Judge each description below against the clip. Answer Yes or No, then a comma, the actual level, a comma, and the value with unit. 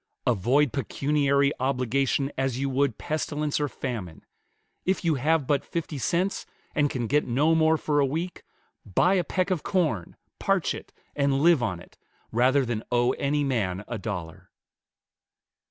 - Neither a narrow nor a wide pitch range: Yes, average, 3.9 semitones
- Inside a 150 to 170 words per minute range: Yes, average, 155 wpm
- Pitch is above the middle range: No, medium, 140 Hz